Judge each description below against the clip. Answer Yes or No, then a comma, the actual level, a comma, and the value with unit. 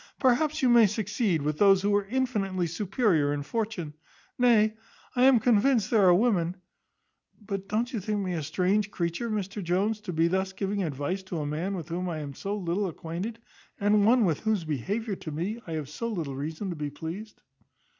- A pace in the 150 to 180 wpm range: No, average, 195 wpm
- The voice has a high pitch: Yes, high, 195 Hz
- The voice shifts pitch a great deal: No, average, 4.4 semitones